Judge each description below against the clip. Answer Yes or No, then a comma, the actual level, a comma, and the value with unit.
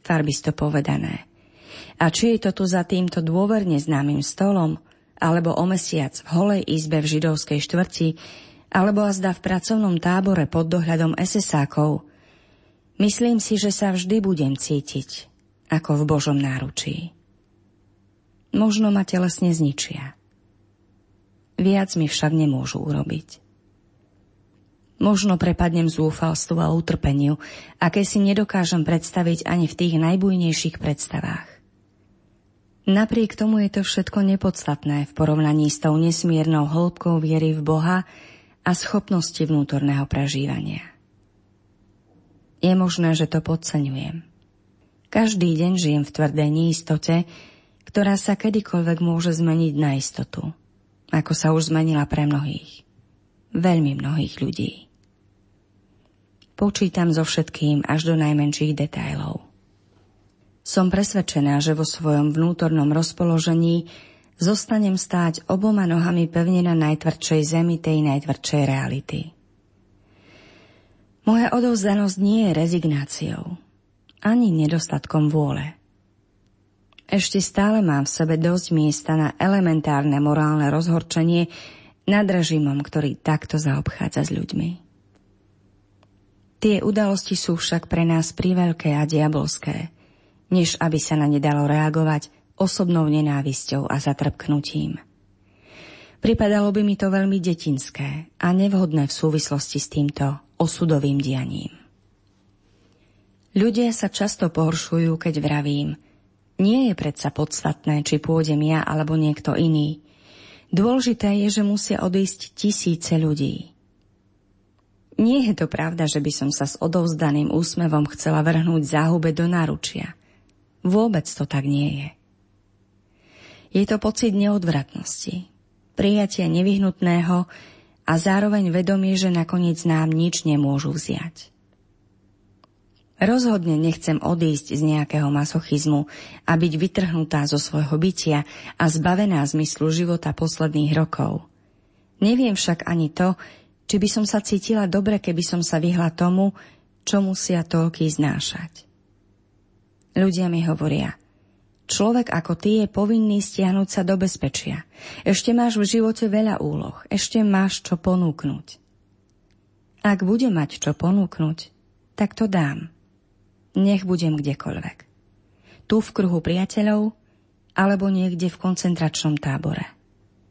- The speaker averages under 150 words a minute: Yes, average, 115 wpm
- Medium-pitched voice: Yes, medium, 160 Hz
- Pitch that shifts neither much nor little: Yes, average, 4.6 semitones